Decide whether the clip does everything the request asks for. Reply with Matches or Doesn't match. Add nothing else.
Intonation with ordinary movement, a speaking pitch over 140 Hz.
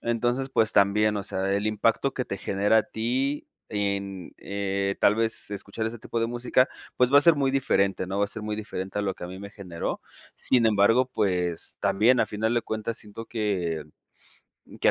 Doesn't match